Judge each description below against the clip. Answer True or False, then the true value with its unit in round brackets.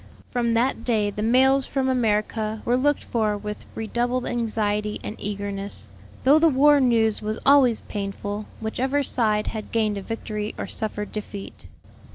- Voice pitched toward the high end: True (220 Hz)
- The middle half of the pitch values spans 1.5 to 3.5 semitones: True (3.1 semitones)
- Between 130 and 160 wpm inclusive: True (155 wpm)